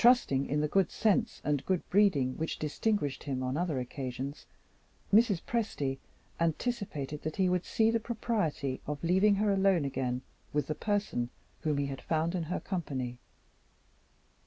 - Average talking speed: Yes, average, 160 wpm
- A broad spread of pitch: Yes, wide, 6.5 semitones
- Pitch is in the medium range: Yes, medium, 160 Hz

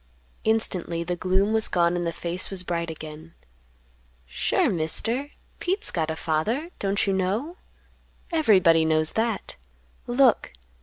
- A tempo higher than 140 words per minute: No, slow, 135 wpm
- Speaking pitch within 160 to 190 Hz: Yes, medium, 185 Hz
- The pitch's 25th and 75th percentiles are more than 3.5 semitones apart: Yes, average, 5.1 semitones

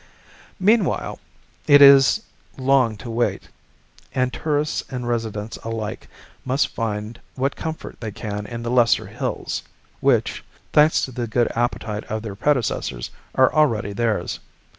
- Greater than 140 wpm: No, slow, 135 wpm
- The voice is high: No, low, 120 Hz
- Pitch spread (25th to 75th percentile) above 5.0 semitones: No, average, 3.9 semitones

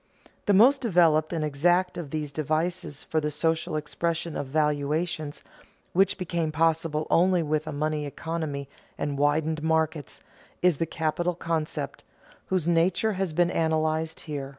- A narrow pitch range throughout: Yes, narrow, 2.2 semitones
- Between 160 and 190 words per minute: No, average, 145 wpm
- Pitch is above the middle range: No, medium, 160 Hz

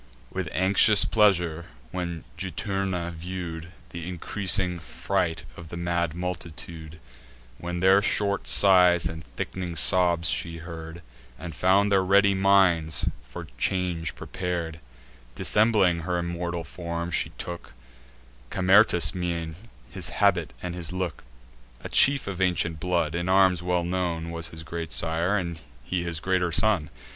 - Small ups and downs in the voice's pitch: Yes, narrow, 1.9 semitones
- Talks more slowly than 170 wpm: Yes, slow, 135 wpm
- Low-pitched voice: Yes, very low, 85 Hz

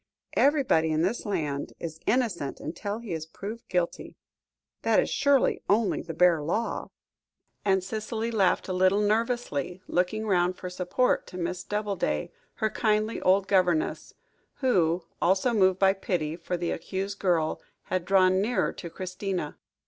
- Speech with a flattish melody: No, average, 3.5 semitones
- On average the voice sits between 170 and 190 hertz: Yes, medium, 185 Hz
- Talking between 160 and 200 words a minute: No, average, 150 wpm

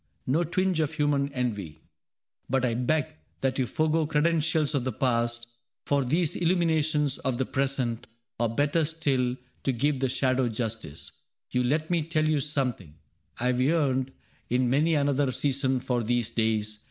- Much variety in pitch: No, average, 3.8 semitones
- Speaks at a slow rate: No, average, 160 wpm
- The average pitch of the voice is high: No, low, 135 Hz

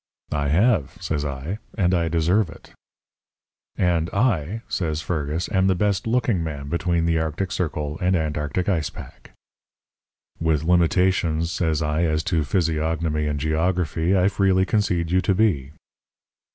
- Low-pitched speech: Yes, very low, 85 Hz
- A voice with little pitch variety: No, average, 3.2 semitones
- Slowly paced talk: No, average, 145 wpm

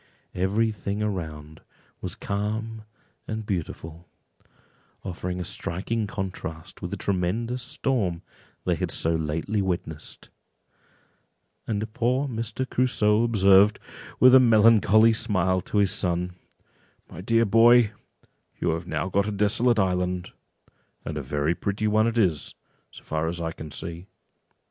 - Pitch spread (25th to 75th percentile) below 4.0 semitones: No, average, 4.3 semitones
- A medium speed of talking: No, slow, 130 wpm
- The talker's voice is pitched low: Yes, low, 100 Hz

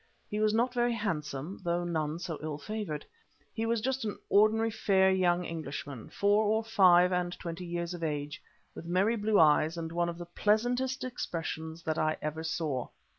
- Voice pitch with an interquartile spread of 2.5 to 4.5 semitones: No, average, 5.0 semitones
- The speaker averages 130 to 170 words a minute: No, average, 180 wpm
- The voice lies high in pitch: No, medium, 175 Hz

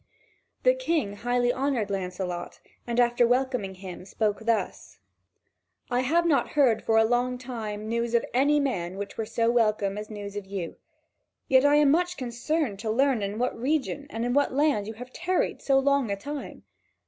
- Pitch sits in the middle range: No, high, 240 Hz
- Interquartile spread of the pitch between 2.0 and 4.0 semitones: No, average, 4.8 semitones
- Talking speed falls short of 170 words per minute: No, average, 185 wpm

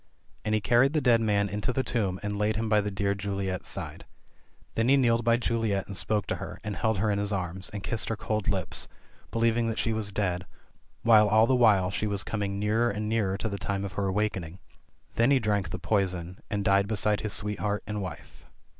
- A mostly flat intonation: Yes, narrow, 2.2 semitones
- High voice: No, low, 105 Hz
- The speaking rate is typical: No, fast, 225 wpm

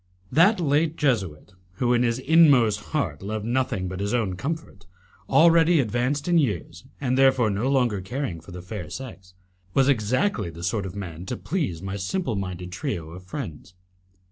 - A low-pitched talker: Yes, low, 110 Hz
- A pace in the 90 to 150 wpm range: No, average, 170 wpm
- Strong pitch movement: Yes, wide, 6.8 semitones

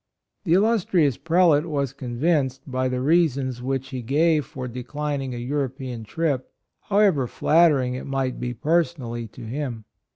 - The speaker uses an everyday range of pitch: Yes, average, 4.0 semitones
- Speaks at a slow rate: No, average, 150 wpm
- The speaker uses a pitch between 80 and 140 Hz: Yes, low, 135 Hz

